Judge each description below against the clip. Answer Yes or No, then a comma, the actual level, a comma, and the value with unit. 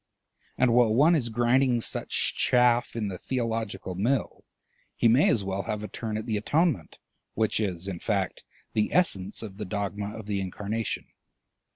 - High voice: No, low, 110 Hz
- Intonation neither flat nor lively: Yes, average, 3.1 semitones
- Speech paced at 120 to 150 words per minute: No, average, 170 wpm